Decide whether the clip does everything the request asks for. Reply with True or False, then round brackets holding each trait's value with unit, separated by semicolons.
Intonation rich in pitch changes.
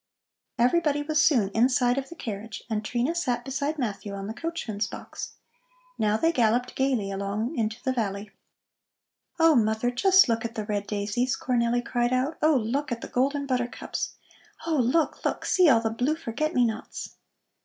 False (4.4 semitones)